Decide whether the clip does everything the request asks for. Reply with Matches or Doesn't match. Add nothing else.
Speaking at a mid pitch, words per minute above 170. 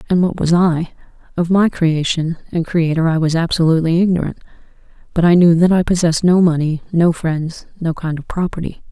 Matches